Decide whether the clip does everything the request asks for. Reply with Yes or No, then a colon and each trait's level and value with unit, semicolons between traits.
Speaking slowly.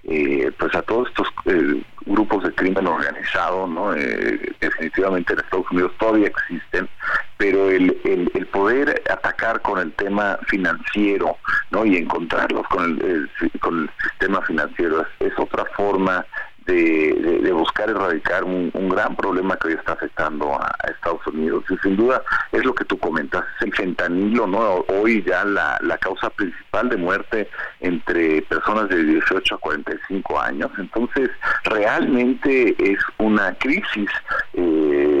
No: average, 155 wpm